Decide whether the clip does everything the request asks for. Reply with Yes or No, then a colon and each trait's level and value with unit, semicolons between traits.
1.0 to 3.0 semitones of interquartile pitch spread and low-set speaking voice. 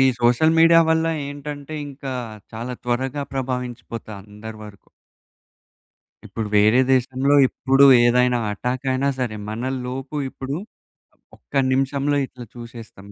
Yes: average, 2.7 semitones; low, 130 Hz